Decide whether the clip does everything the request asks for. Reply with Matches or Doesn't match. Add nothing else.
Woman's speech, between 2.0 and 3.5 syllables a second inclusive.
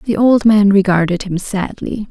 Doesn't match